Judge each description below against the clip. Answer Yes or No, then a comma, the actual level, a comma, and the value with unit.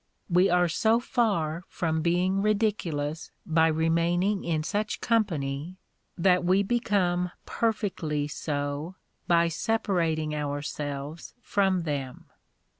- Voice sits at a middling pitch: Yes, medium, 170 Hz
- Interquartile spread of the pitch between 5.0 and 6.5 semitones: No, average, 4.2 semitones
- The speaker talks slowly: Yes, slow, 105 wpm